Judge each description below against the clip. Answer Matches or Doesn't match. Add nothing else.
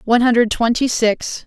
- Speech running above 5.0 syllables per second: Matches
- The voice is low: Doesn't match